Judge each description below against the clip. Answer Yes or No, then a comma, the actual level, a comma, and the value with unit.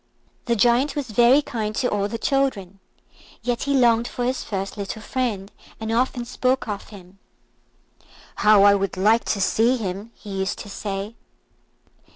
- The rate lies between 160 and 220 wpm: Yes, average, 165 wpm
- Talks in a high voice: Yes, high, 220 Hz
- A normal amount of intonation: Yes, average, 3.6 semitones